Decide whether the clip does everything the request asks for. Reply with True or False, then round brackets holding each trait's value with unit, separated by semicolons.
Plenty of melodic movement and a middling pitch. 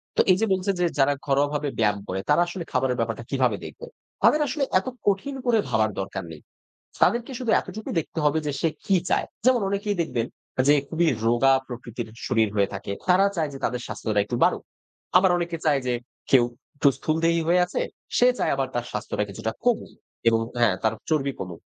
True (7.8 semitones; 145 Hz)